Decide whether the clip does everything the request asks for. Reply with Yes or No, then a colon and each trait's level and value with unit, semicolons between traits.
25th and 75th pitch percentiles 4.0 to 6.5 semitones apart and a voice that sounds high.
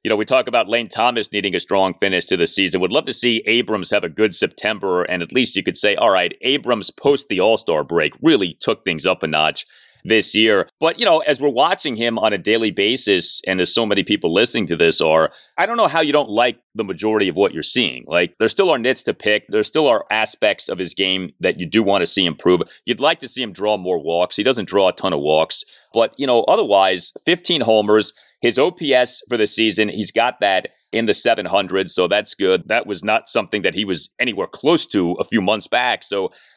No: average, 4.6 semitones; low, 110 Hz